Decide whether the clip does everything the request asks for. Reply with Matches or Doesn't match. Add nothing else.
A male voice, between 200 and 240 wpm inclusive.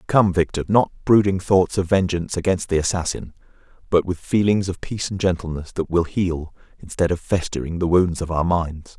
Doesn't match